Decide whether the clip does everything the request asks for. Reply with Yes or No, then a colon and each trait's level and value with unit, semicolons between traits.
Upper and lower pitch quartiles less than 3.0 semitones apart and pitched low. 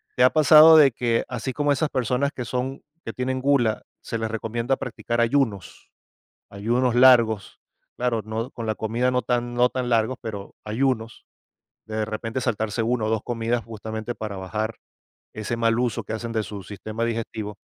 Yes: narrow, 2.4 semitones; low, 115 Hz